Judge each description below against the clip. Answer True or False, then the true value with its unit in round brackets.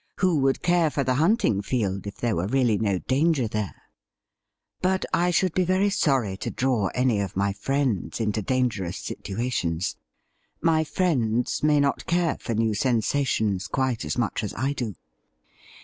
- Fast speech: False (165 wpm)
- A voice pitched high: False (125 Hz)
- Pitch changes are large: True (6.2 semitones)